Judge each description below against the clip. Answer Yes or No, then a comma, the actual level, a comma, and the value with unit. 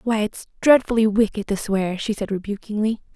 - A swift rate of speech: No, average, 170 wpm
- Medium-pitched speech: No, high, 210 Hz